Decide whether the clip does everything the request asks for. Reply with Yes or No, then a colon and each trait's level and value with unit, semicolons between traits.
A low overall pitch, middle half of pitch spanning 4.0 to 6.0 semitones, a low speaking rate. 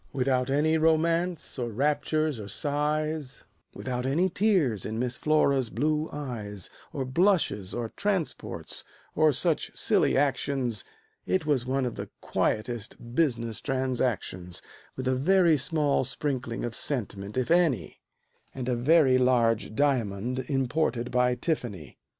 Yes: low, 130 Hz; average, 4.3 semitones; slow, 130 wpm